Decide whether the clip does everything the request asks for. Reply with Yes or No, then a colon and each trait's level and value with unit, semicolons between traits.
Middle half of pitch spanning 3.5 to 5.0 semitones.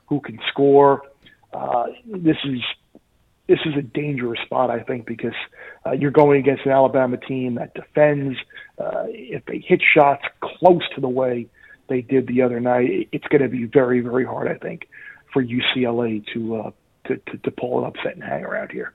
No: average, 2.7 semitones